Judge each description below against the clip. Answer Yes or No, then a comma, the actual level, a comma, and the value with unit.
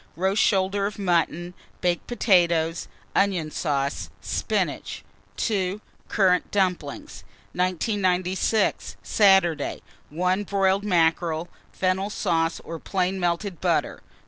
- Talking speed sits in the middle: No, slow, 95 wpm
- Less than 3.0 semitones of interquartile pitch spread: Yes, narrow, 2.5 semitones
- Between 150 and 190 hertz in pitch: Yes, medium, 185 Hz